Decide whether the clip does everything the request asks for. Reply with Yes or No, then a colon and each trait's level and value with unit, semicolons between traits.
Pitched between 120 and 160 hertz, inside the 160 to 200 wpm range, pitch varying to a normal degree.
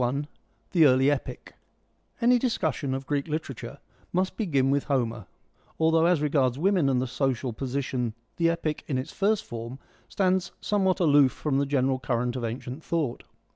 Yes: medium, 140 Hz; average, 170 wpm; average, 4.4 semitones